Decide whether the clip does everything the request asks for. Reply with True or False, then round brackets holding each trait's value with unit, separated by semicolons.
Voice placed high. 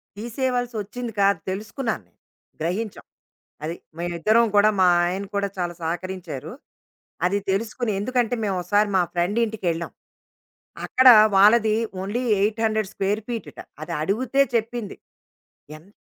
True (205 Hz)